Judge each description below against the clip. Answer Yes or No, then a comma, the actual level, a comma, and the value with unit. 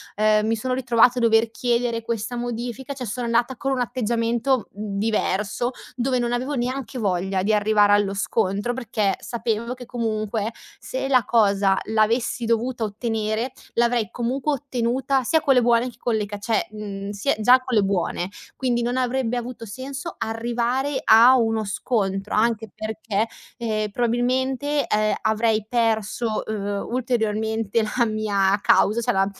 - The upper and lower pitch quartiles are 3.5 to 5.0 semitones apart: No, narrow, 2.5 semitones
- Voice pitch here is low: No, high, 230 Hz